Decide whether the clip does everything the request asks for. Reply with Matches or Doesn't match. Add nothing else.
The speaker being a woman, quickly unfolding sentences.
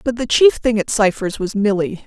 Matches